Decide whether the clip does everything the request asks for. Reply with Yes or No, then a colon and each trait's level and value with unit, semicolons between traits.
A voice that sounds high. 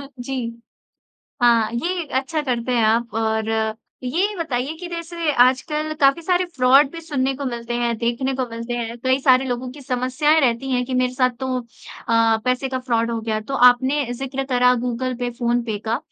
Yes: very high, 255 Hz